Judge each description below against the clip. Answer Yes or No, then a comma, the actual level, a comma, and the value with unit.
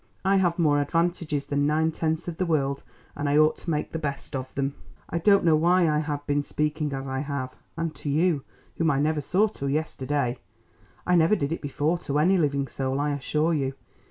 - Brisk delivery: Yes, fast, 215 wpm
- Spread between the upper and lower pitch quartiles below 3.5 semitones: Yes, average, 2.8 semitones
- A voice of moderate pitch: Yes, medium, 150 Hz